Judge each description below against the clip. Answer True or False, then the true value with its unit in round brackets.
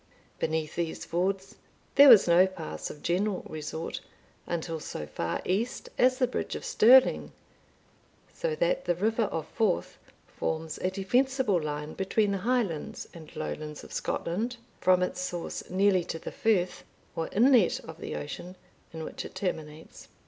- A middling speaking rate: True (155 wpm)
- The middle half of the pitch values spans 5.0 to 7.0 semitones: True (5.4 semitones)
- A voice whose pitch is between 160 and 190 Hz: True (185 Hz)